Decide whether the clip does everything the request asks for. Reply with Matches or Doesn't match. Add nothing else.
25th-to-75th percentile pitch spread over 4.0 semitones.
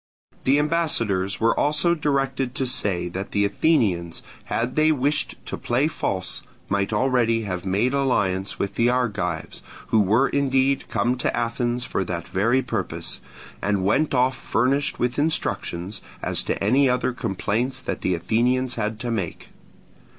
Matches